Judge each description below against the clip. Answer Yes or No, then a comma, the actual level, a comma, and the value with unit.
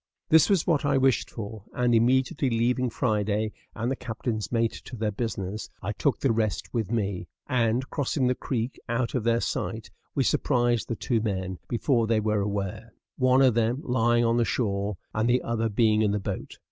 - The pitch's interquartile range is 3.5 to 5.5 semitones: No, average, 2.7 semitones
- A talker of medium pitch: No, low, 115 Hz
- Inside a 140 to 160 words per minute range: No, average, 195 wpm